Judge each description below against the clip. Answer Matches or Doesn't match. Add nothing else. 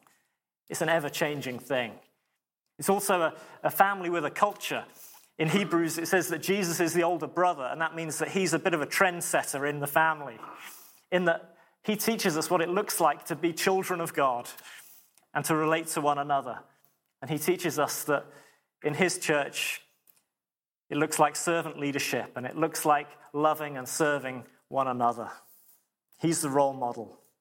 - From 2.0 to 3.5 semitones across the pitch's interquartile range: Matches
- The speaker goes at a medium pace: Matches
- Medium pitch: Matches